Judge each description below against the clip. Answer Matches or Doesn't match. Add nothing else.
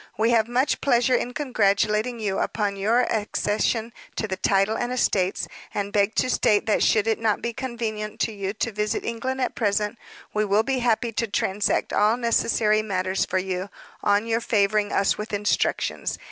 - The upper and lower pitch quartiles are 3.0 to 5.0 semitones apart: Doesn't match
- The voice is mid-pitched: Doesn't match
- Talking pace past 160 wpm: Matches